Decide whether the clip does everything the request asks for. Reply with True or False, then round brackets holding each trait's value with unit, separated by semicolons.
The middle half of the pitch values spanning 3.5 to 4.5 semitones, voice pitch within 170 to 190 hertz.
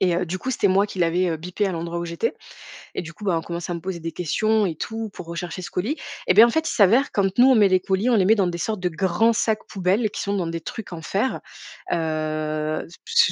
True (4.2 semitones; 185 Hz)